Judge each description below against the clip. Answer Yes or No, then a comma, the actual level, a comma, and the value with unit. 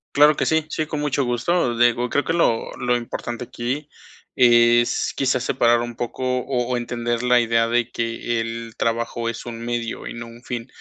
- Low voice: Yes, low, 120 Hz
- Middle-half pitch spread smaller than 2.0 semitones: Yes, narrow, 1.2 semitones